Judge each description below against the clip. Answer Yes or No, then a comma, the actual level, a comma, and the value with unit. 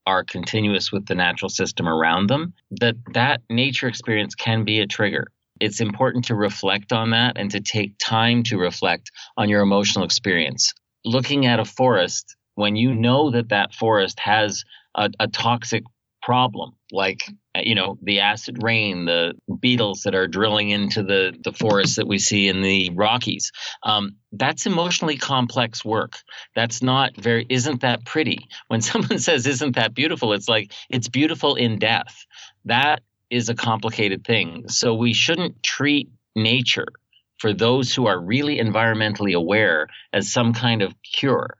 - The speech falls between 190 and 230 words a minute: No, average, 165 wpm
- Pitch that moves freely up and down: No, average, 3.4 semitones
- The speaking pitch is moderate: No, low, 115 Hz